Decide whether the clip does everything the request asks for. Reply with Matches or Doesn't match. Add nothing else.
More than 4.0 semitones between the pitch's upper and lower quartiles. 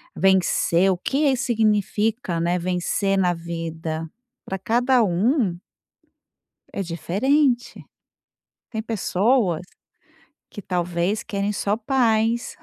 Matches